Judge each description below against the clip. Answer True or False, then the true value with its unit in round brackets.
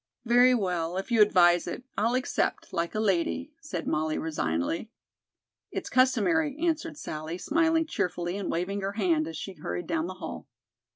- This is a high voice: True (200 Hz)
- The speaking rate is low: False (165 wpm)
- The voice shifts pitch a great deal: True (7.3 semitones)